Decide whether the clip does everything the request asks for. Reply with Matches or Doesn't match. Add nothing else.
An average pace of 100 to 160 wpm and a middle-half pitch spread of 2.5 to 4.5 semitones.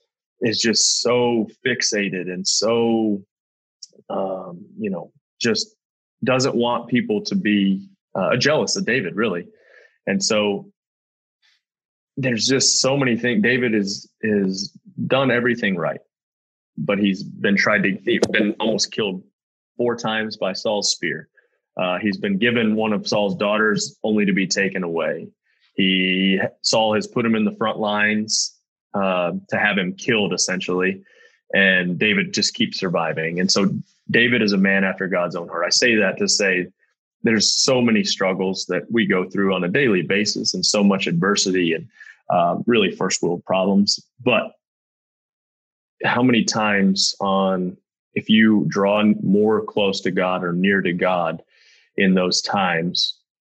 Matches